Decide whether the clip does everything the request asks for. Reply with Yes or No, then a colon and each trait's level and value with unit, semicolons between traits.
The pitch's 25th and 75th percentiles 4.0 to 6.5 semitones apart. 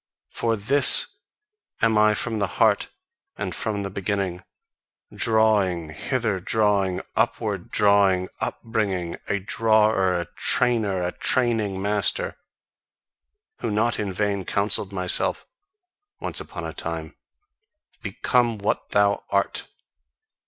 No: narrow, 2.5 semitones